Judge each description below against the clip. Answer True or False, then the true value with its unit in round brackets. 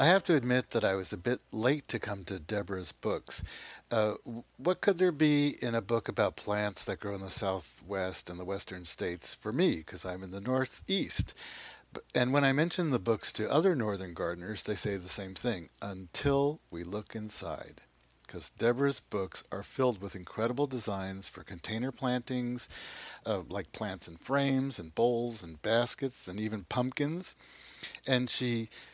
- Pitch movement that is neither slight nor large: True (5.0 semitones)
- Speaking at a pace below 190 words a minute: True (175 wpm)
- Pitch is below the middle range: True (110 Hz)